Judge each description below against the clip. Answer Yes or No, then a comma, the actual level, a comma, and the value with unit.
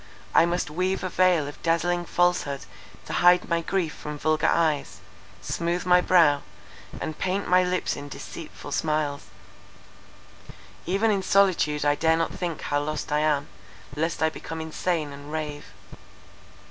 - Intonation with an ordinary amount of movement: Yes, average, 3.1 semitones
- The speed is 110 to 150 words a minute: Yes, average, 145 wpm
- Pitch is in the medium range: Yes, medium, 165 Hz